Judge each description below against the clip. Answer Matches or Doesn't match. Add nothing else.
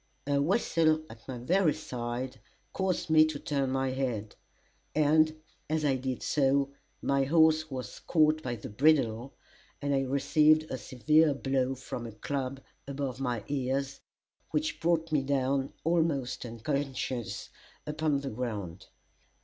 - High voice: Doesn't match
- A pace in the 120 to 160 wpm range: Matches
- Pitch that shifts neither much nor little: Matches